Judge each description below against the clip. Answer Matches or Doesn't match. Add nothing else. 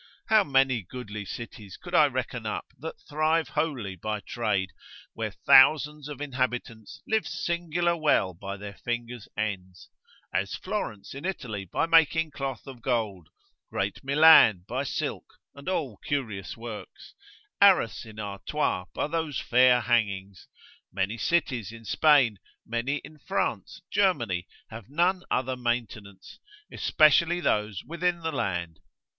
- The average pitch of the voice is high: Doesn't match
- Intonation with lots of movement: Matches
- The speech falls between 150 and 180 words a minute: Doesn't match